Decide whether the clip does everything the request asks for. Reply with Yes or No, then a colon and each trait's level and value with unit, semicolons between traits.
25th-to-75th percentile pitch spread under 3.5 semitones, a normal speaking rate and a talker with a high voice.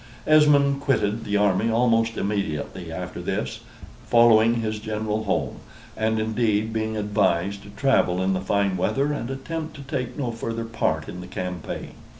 No: average, 2.8 semitones; average, 160 wpm; low, 110 Hz